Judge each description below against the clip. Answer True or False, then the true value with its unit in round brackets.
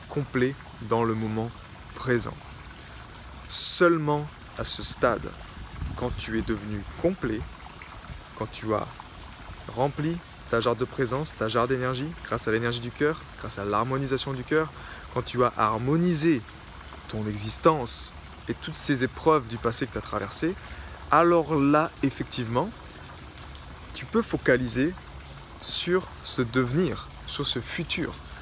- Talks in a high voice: False (120 Hz)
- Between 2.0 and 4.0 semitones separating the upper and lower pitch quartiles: False (5.4 semitones)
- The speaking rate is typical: False (135 wpm)